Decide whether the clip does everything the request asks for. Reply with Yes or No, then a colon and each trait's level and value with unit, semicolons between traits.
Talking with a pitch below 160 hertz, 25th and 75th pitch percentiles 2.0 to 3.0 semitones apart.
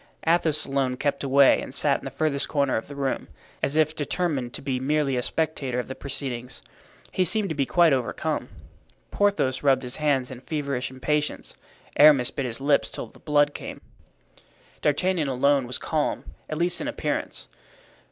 Yes: medium, 140 Hz; average, 2.7 semitones